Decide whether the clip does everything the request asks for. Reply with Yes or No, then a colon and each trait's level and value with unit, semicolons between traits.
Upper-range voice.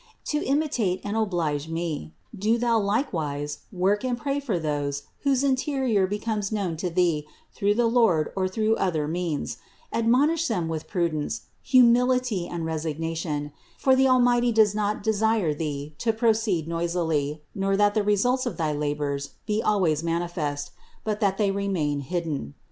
Yes: high, 195 Hz